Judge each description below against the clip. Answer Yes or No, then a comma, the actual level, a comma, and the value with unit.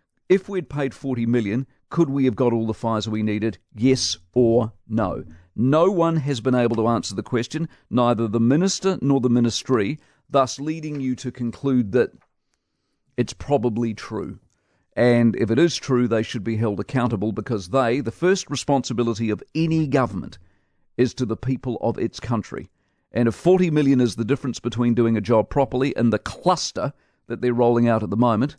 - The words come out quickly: No, average, 185 wpm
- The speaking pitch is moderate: No, low, 120 Hz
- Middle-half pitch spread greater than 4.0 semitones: No, average, 3.4 semitones